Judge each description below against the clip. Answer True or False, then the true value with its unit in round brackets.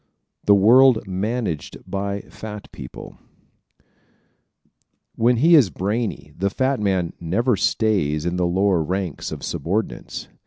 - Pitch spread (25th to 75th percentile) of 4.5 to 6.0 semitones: False (4.1 semitones)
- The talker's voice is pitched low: True (100 Hz)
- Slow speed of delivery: True (125 wpm)